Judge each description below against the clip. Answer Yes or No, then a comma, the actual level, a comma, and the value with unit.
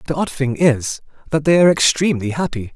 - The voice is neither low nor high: Yes, medium, 145 Hz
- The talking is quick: No, average, 195 wpm